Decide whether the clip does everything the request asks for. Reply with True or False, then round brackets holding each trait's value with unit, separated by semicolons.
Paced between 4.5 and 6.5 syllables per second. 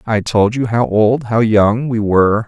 False (4.3 syllables/s)